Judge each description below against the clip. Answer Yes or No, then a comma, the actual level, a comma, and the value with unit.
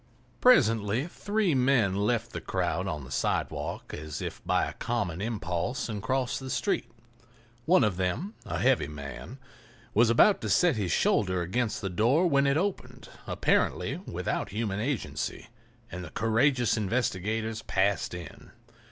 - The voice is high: No, low, 110 Hz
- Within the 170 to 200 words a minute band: No, average, 150 wpm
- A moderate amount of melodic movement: No, wide, 5.9 semitones